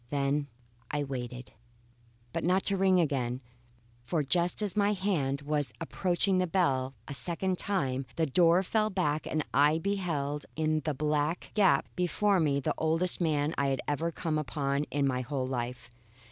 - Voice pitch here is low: No, medium, 155 Hz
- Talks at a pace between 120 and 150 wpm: No, average, 165 wpm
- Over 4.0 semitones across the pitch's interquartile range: Yes, average, 4.5 semitones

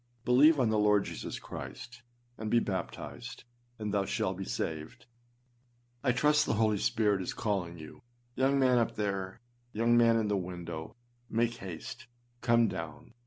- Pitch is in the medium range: No, low, 110 Hz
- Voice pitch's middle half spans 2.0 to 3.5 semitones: No, average, 3.9 semitones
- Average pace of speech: Yes, average, 160 wpm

